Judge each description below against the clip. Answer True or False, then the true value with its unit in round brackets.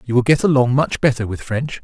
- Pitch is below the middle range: True (130 Hz)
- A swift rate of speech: True (260 wpm)